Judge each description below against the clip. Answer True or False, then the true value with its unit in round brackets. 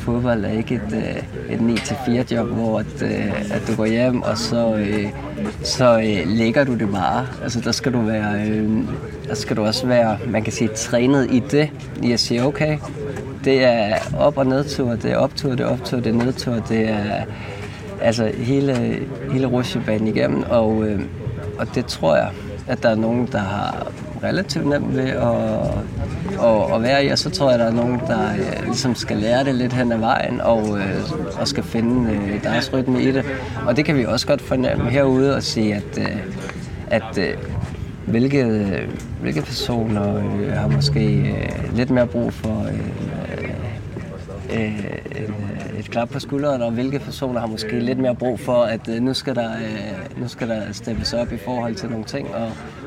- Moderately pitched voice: False (115 Hz)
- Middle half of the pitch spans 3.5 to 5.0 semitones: False (2.9 semitones)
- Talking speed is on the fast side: False (180 wpm)